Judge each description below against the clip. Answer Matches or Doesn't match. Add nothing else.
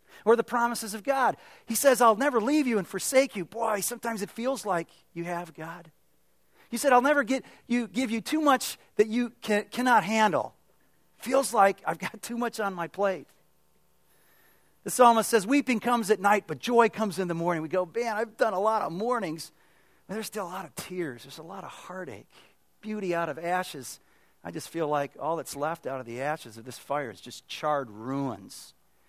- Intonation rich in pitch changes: Matches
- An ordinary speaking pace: Doesn't match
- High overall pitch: Matches